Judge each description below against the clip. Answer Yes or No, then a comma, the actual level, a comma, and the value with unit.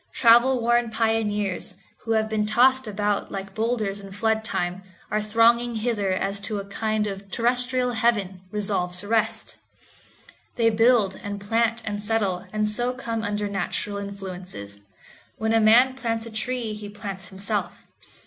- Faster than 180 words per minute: No, average, 160 wpm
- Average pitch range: No, narrow, 2.3 semitones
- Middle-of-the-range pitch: No, high, 215 Hz